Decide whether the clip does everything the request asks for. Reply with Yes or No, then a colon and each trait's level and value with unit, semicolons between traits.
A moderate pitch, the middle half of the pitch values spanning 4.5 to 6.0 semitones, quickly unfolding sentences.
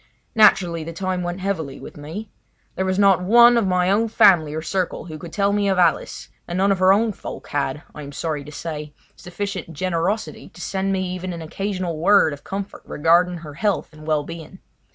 No: medium, 180 Hz; average, 3.6 semitones; fast, 210 wpm